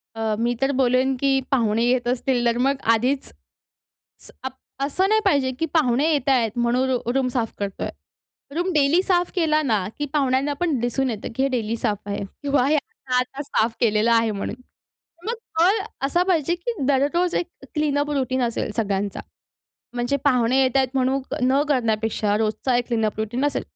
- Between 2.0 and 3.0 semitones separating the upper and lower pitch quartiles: No, average, 3.6 semitones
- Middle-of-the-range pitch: No, very high, 260 Hz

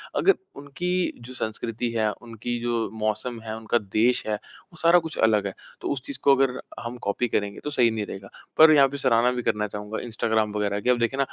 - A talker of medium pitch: No, low, 115 Hz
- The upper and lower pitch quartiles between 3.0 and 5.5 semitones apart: Yes, average, 3.3 semitones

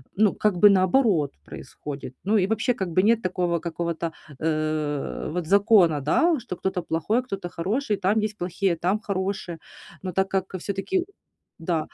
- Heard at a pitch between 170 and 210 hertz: Yes, medium, 185 Hz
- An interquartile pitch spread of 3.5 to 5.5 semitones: Yes, average, 3.8 semitones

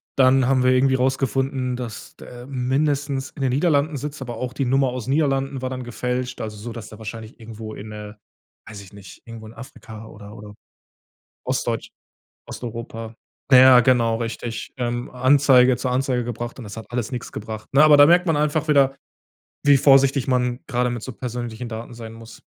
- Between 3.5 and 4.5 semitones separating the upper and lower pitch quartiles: No, average, 2.8 semitones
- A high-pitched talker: No, low, 125 Hz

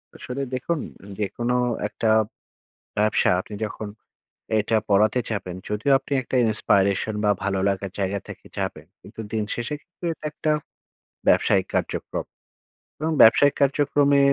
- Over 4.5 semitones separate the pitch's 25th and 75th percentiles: Yes, average, 5.3 semitones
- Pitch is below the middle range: Yes, low, 110 Hz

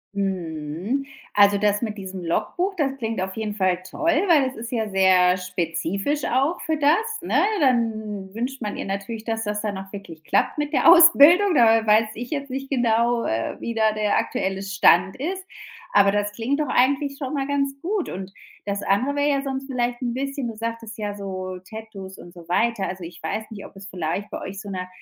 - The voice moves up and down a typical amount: No, wide, 5.7 semitones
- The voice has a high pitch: Yes, high, 220 Hz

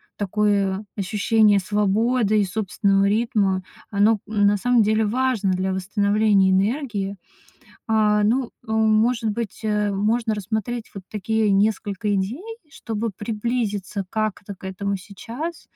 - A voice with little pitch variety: Yes, narrow, 1.9 semitones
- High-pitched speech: Yes, high, 210 Hz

